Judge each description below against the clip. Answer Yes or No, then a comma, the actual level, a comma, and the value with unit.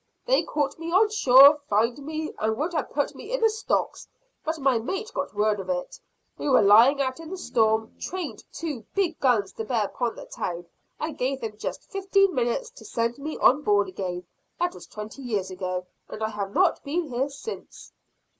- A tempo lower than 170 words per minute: No, average, 200 wpm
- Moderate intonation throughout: No, wide, 7.1 semitones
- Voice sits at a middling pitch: No, very high, 265 Hz